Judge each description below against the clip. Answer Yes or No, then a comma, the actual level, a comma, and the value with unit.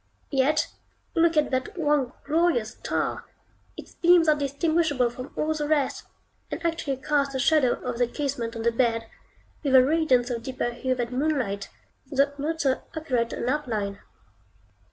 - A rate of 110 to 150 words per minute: No, average, 160 wpm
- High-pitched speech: Yes, very high, 275 Hz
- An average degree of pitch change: Yes, average, 3.9 semitones